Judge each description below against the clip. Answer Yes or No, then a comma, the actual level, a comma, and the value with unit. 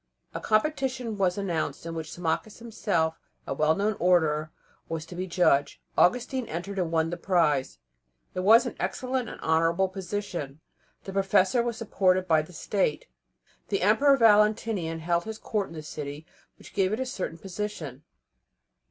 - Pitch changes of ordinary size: Yes, average, 4.7 semitones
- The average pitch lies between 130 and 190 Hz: Yes, medium, 185 Hz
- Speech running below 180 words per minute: Yes, average, 165 wpm